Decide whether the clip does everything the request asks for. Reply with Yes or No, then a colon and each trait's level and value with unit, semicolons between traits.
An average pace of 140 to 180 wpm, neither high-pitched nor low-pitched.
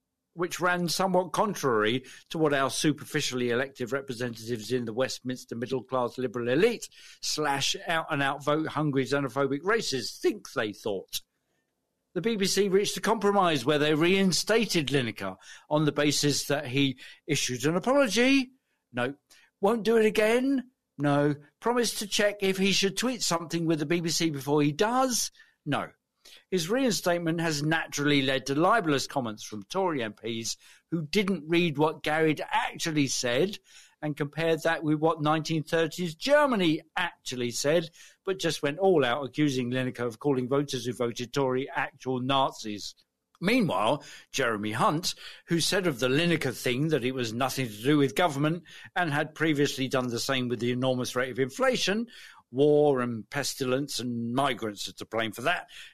Yes: average, 160 wpm; medium, 150 Hz